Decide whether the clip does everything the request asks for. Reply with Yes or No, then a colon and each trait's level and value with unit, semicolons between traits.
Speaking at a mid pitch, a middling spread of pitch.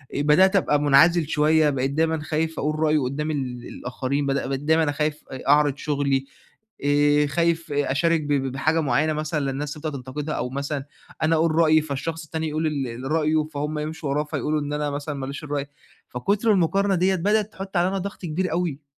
No: medium, 150 Hz; narrow, 2.2 semitones